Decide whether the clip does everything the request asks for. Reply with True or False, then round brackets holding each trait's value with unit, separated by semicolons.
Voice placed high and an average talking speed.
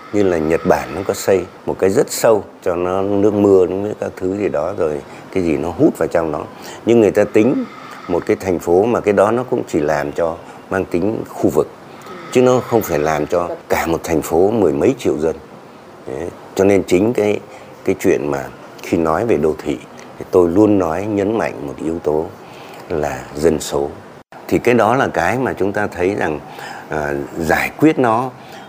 False (100 Hz; 210 wpm)